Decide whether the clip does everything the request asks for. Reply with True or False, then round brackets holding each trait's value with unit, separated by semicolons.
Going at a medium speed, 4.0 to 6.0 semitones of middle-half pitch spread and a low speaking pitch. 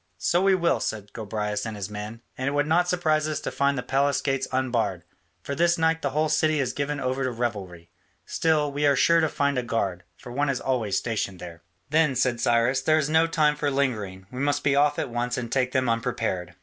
False (230 wpm; 4.4 semitones; 130 Hz)